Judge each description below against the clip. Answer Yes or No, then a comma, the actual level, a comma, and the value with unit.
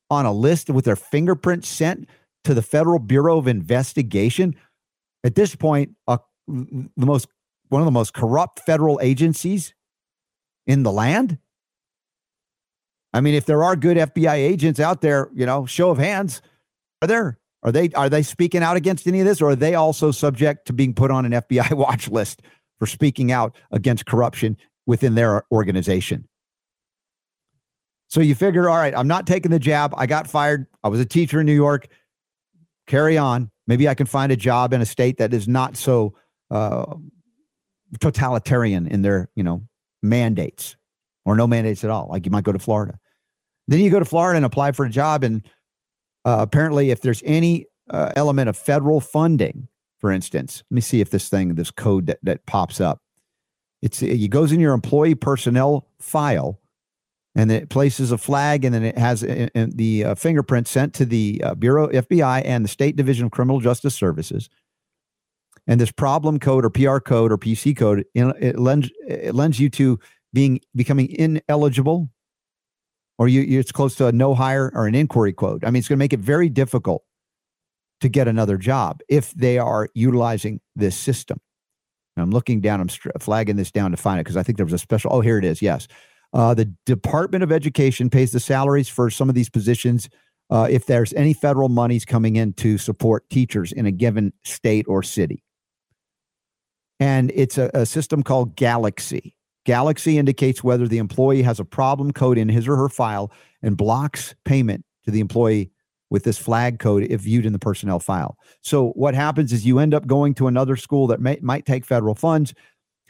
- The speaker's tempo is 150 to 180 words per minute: No, average, 190 wpm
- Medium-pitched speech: No, low, 130 Hz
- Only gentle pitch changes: No, average, 4.3 semitones